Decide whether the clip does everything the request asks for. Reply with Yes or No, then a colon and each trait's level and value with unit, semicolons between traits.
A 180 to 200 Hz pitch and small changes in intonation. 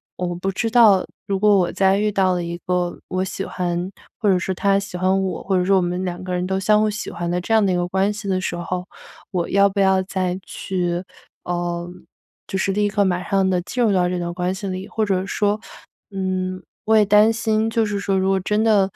Yes: high, 190 Hz; narrow, 1.9 semitones